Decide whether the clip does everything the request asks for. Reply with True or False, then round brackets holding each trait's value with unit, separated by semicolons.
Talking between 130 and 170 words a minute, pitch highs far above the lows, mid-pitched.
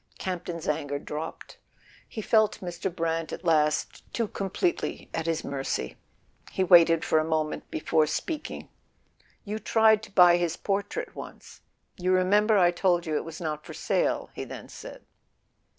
False (150 wpm; 3.9 semitones; 175 Hz)